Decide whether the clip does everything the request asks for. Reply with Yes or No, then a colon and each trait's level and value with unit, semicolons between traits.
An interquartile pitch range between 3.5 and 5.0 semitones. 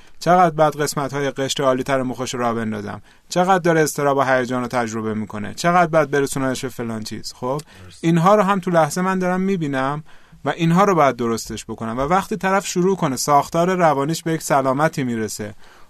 No: wide, 5.6 semitones